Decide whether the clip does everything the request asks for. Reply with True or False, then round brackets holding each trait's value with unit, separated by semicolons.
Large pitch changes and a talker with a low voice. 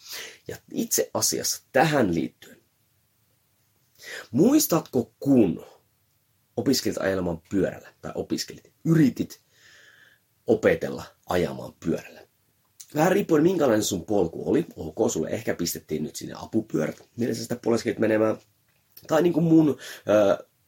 True (7.2 semitones; 120 Hz)